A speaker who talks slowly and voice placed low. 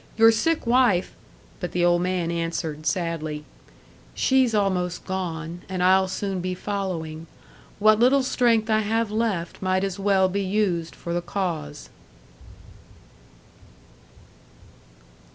No: slow, 125 wpm; medium, 185 Hz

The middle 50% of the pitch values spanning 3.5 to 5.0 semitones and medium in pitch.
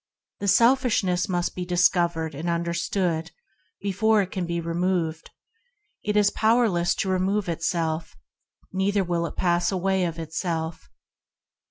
No: narrow, 2.4 semitones; medium, 180 Hz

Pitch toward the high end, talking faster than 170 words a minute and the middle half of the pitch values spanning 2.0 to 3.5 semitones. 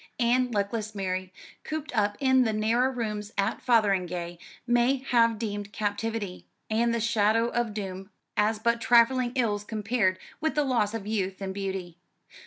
No: high, 220 Hz; average, 155 wpm; average, 2.8 semitones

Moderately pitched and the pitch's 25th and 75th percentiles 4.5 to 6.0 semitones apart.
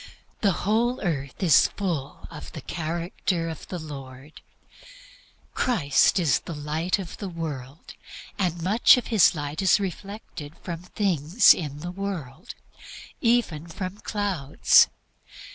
Yes: medium, 170 Hz; average, 4.8 semitones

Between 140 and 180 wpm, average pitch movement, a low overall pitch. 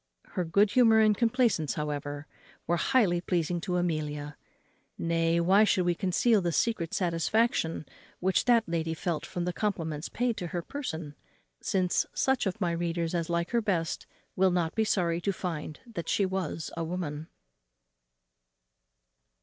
No: average, 155 wpm; average, 3.6 semitones; medium, 175 Hz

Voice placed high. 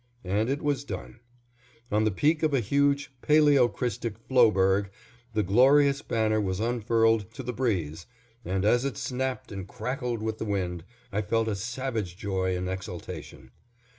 No: low, 110 Hz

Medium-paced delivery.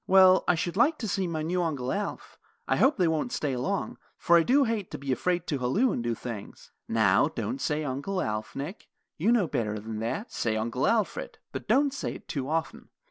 No: fast, 220 wpm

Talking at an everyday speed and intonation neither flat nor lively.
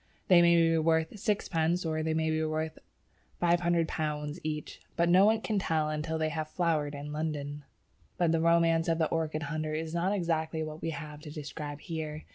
No: average, 190 wpm; narrow, 1.5 semitones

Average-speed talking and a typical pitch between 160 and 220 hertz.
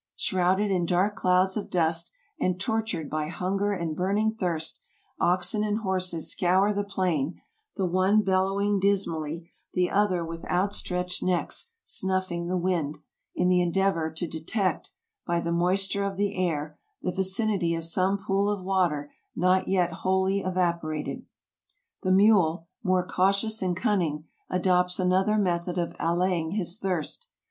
Yes: average, 145 wpm; medium, 185 Hz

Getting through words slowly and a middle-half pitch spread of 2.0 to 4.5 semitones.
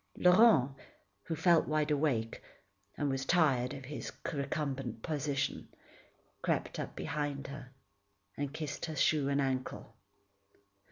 Yes: slow, 120 wpm; narrow, 2.4 semitones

